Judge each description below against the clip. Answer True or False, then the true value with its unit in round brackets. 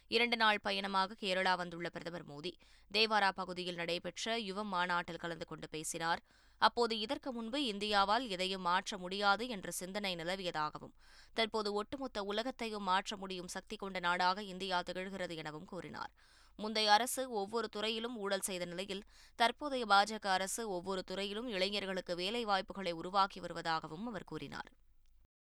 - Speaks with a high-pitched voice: True (195 Hz)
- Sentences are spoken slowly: False (130 wpm)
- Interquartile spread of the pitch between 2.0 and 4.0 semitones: True (3.5 semitones)